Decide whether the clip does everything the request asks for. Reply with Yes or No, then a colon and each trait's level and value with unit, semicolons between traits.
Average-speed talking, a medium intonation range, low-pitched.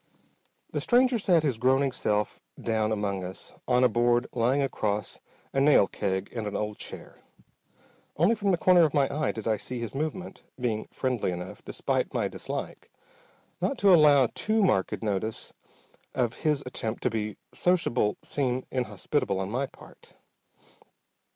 No: average, 155 wpm; wide, 5.9 semitones; low, 125 Hz